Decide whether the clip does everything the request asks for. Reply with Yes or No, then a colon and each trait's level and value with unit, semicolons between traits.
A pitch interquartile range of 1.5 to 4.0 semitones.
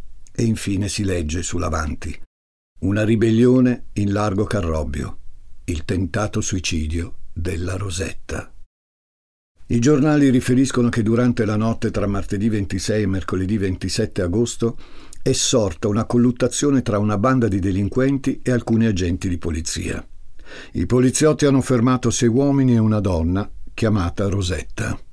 No: average, 4.7 semitones